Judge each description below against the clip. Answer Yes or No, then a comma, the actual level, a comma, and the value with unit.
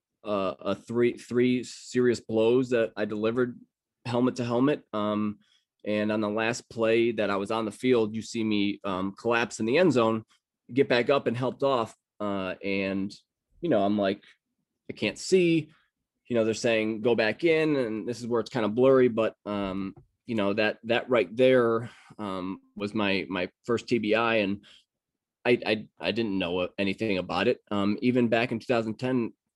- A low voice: Yes, low, 110 Hz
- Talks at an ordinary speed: Yes, average, 185 wpm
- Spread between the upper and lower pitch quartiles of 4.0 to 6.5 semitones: No, average, 2.9 semitones